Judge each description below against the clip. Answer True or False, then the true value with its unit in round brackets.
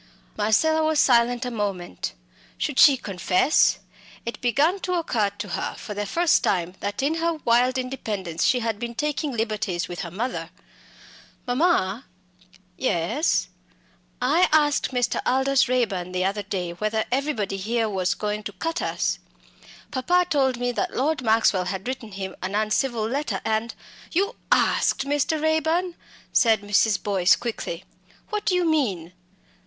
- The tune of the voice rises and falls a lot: True (6.1 semitones)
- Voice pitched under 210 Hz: False (235 Hz)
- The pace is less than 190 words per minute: True (155 wpm)